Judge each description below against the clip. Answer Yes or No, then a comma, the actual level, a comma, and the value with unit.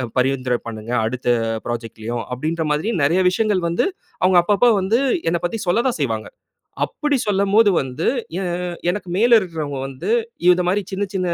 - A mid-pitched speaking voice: Yes, medium, 170 Hz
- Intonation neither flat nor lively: No, wide, 7.7 semitones